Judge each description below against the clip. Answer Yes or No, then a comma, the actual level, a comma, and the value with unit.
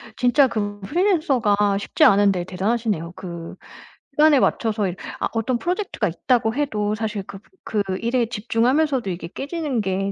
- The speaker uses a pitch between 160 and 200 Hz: No, high, 225 Hz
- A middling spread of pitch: Yes, average, 4.9 semitones